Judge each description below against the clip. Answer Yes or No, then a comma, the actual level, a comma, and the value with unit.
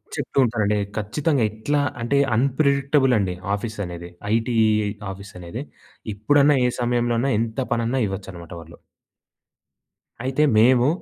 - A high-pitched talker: No, low, 115 Hz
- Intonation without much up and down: No, average, 4.8 semitones